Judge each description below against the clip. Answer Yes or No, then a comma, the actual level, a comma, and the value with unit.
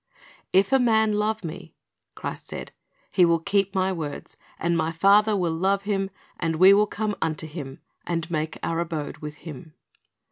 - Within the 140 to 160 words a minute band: No, average, 175 wpm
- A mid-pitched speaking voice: Yes, medium, 175 Hz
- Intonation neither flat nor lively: Yes, average, 3.8 semitones